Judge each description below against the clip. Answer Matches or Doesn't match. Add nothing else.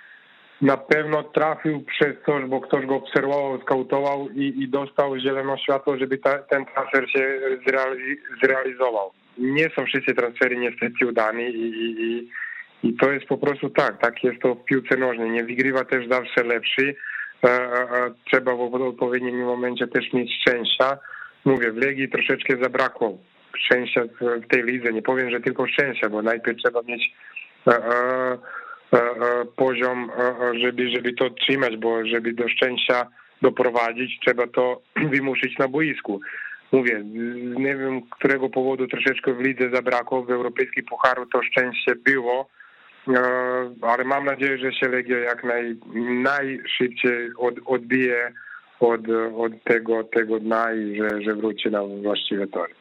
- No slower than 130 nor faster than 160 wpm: Matches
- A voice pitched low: Matches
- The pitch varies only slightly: Matches